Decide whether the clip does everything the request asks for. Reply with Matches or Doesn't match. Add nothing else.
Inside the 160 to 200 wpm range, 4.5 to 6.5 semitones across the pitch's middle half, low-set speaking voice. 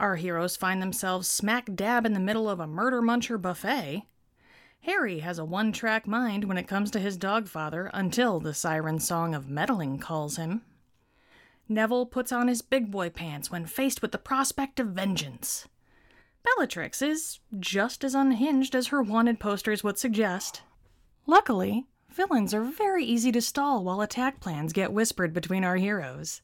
Doesn't match